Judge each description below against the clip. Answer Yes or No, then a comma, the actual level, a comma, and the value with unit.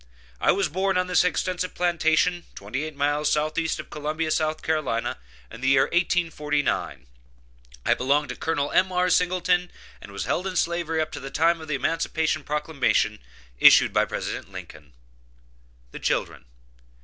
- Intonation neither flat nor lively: Yes, average, 3.3 semitones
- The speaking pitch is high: No, medium, 155 Hz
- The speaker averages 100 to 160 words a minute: Yes, average, 155 wpm